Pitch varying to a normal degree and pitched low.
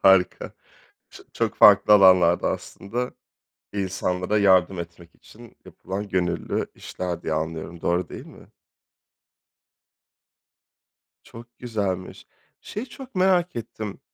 Yes: average, 4.2 semitones; very low, 95 Hz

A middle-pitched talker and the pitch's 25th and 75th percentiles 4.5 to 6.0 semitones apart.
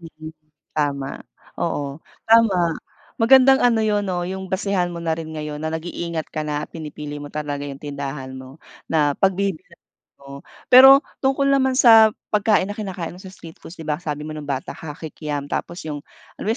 Yes: medium, 160 Hz; average, 5.2 semitones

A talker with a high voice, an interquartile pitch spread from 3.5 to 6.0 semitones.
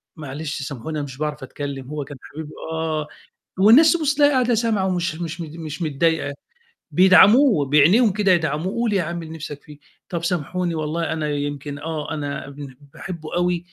No: medium, 160 Hz; average, 3.9 semitones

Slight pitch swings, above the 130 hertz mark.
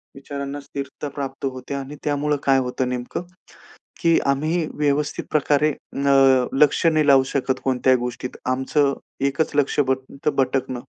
Yes: narrow, 1.8 semitones; medium, 140 Hz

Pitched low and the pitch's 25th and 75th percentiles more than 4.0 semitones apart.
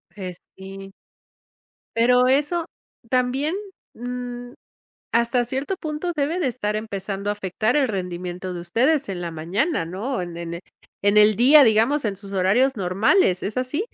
No: high, 225 Hz; wide, 5.6 semitones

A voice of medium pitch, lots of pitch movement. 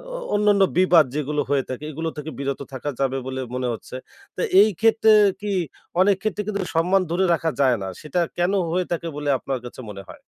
Yes: medium, 160 Hz; wide, 6.0 semitones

